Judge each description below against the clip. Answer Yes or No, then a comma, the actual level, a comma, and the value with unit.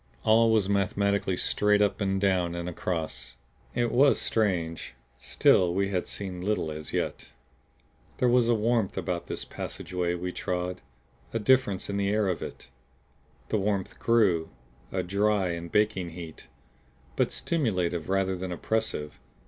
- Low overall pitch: Yes, very low, 95 Hz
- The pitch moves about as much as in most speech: Yes, average, 3.1 semitones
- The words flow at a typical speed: Yes, average, 150 wpm